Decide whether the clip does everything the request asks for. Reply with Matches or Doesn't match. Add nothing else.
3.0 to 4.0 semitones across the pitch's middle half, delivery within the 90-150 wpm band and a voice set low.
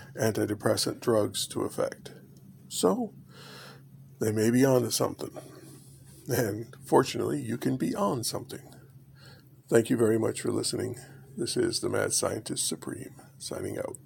Matches